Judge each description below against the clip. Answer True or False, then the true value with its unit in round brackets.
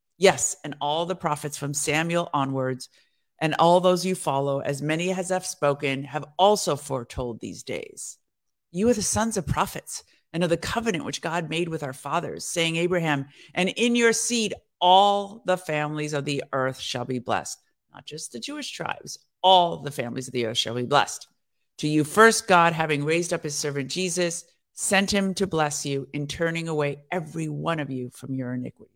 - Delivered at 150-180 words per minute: False (195 wpm)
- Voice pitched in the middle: True (160 Hz)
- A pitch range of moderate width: True (4.4 semitones)